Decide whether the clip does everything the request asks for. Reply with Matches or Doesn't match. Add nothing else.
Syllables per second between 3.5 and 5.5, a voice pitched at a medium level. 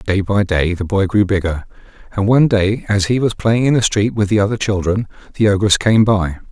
Doesn't match